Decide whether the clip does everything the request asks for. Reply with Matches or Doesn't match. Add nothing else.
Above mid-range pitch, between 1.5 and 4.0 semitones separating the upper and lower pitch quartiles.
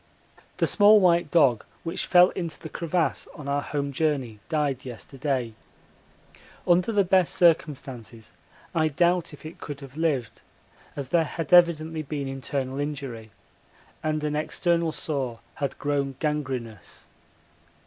Doesn't match